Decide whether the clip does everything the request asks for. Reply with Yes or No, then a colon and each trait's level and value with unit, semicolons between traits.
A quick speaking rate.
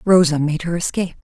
No: average, 195 wpm